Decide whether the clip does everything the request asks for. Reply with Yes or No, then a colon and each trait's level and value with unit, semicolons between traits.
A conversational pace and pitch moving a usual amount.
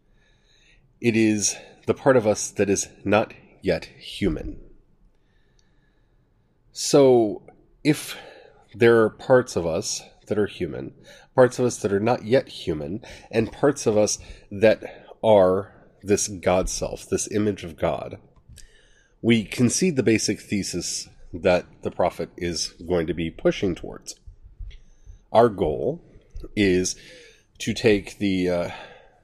No: slow, 130 wpm; average, 4.6 semitones